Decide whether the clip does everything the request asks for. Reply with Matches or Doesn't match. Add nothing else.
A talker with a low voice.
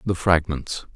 Matches